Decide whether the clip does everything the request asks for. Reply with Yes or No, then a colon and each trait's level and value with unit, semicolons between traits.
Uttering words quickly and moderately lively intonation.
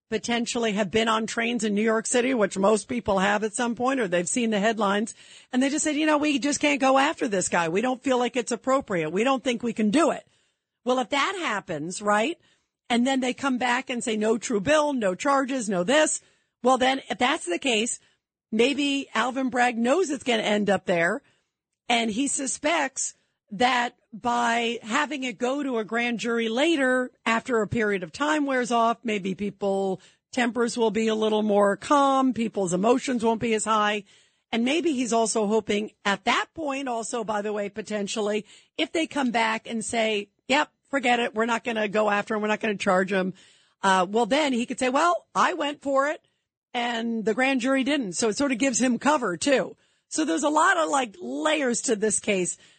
Yes: fast, 210 wpm; average, 3.9 semitones